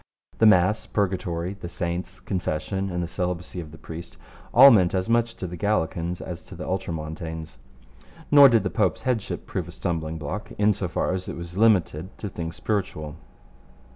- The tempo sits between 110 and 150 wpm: No, average, 180 wpm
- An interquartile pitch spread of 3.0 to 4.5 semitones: Yes, average, 3.4 semitones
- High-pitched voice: No, very low, 90 Hz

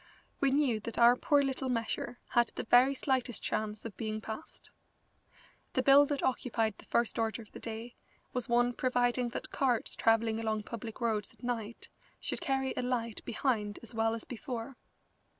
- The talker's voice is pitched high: Yes, high, 235 Hz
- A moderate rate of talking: Yes, average, 175 wpm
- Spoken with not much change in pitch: Yes, narrow, 2.3 semitones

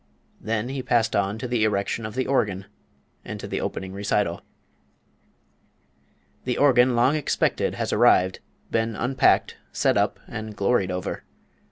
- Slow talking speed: No, average, 145 wpm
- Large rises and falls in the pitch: No, average, 3.9 semitones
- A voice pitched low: Yes, low, 110 Hz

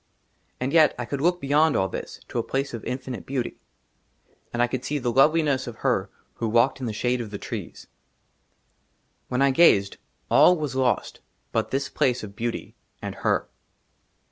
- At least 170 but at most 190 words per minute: Yes, average, 180 wpm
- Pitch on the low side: Yes, low, 130 Hz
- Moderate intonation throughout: Yes, average, 3.0 semitones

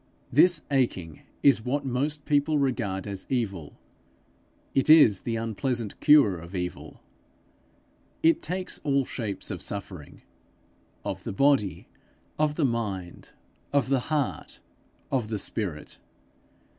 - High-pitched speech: No, low, 125 Hz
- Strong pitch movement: Yes, wide, 6.3 semitones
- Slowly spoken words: Yes, slow, 120 wpm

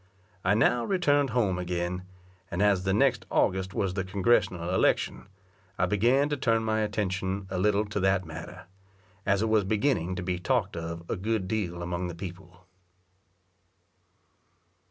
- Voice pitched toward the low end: Yes, very low, 95 Hz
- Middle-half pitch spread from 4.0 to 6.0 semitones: No, average, 3.3 semitones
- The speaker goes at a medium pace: Yes, average, 155 wpm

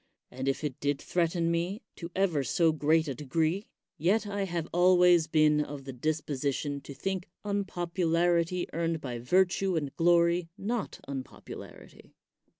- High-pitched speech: No, medium, 165 Hz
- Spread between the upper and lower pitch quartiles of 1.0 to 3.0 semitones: No, average, 3.4 semitones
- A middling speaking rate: Yes, average, 150 wpm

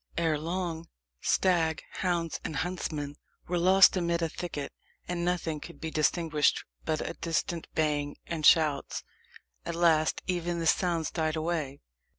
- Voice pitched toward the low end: No, medium, 165 Hz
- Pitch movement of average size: No, narrow, 1.9 semitones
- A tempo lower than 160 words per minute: Yes, average, 145 wpm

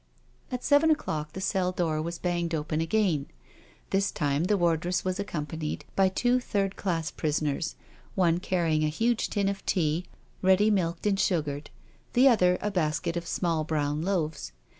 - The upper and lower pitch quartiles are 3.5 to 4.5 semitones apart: Yes, average, 3.9 semitones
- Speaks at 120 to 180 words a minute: Yes, average, 160 wpm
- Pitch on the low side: No, medium, 175 Hz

